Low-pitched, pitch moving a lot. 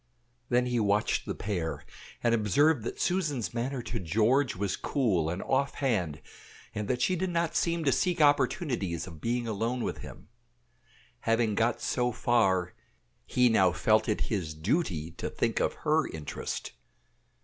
Yes: low, 115 Hz; wide, 5.7 semitones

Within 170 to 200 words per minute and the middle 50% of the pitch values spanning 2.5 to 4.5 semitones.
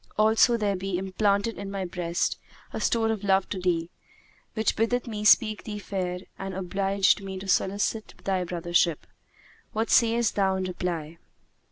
No: average, 160 wpm; average, 2.8 semitones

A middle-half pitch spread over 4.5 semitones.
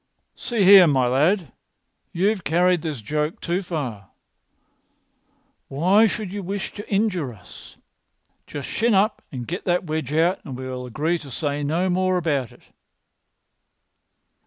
Yes: average, 5.0 semitones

